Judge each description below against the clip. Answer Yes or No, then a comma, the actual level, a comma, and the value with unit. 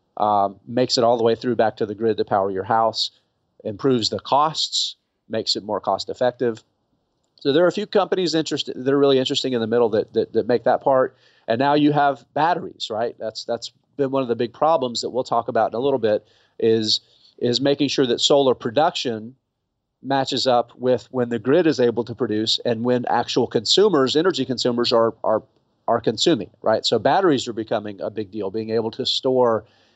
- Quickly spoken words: Yes, fast, 210 wpm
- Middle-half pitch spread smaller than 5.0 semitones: Yes, average, 3.0 semitones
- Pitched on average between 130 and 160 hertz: No, low, 120 Hz